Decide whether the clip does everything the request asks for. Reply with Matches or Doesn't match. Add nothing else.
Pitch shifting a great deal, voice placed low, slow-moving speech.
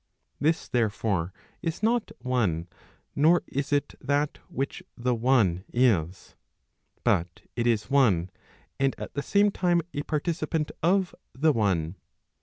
Matches